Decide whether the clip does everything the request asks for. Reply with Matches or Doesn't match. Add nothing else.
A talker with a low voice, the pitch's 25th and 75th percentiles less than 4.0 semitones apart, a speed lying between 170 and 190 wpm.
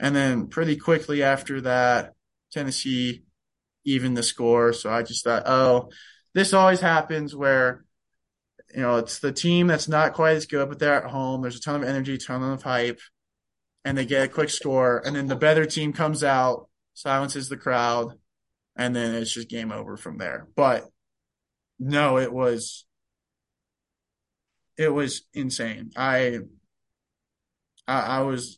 Doesn't match